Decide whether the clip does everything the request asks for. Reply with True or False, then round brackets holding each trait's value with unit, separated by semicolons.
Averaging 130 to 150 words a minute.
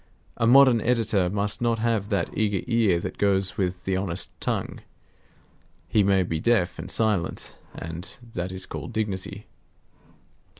True (145 wpm)